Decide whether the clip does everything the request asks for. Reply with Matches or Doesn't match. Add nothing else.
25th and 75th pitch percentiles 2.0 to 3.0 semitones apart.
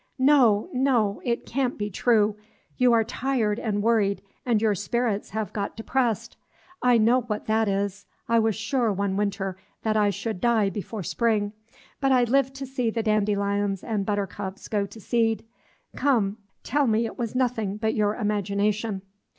Matches